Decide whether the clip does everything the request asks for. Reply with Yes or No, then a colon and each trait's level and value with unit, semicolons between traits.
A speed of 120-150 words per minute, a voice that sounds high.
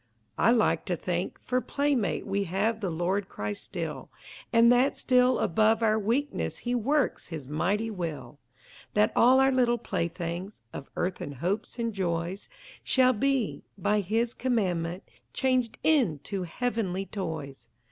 Yes: average, 140 wpm; high, 205 Hz